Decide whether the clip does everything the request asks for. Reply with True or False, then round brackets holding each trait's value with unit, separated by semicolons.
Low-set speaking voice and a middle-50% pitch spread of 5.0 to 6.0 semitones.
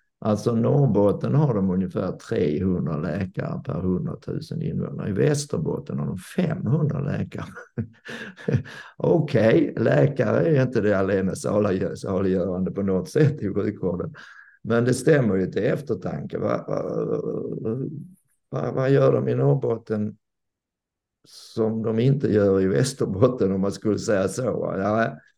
True (110 Hz; 5.5 semitones)